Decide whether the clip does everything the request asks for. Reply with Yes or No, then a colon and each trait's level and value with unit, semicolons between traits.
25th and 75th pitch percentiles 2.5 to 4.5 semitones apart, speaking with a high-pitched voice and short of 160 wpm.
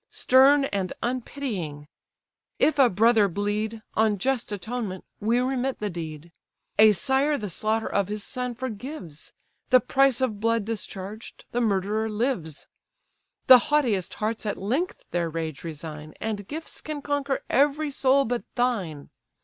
No: average, 5.1 semitones; high, 220 Hz; average, 140 wpm